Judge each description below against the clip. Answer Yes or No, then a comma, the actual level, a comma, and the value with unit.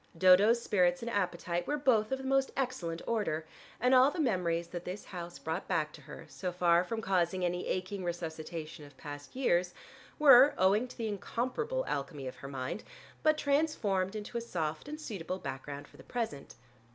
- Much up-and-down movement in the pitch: Yes, wide, 6.1 semitones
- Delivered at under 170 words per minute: No, average, 185 wpm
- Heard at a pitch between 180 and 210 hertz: Yes, medium, 185 Hz